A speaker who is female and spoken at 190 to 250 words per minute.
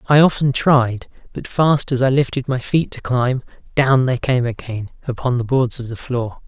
No: male; fast, 205 wpm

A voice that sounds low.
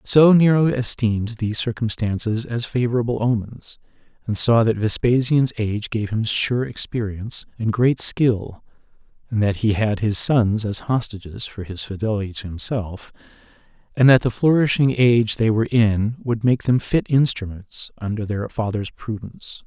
Yes: low, 115 Hz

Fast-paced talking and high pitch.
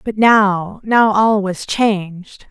No: average, 145 wpm; high, 205 Hz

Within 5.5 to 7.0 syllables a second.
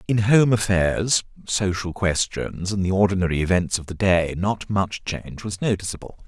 No: 4.8 syllables/s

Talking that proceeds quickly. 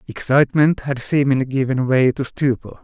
No: average, 150 wpm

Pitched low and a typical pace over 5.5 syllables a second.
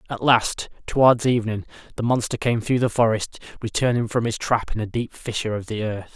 Yes: low, 115 Hz; 5.8 syllables/s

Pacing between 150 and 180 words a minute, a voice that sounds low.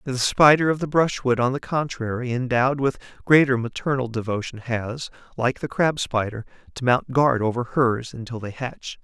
Yes: average, 175 wpm; low, 125 Hz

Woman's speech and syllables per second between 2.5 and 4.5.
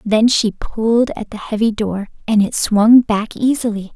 Yes: female; 4.4 syllables/s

